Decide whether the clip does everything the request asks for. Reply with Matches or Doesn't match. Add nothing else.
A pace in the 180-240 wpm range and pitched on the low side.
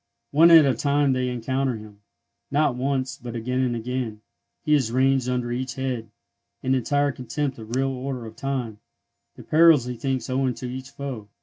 Matches